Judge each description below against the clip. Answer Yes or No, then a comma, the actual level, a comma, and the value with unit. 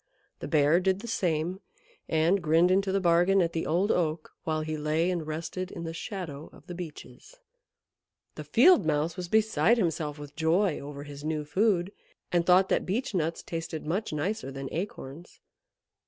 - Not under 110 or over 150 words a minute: No, average, 175 wpm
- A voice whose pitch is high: No, medium, 170 Hz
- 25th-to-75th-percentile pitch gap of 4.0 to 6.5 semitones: No, average, 3.3 semitones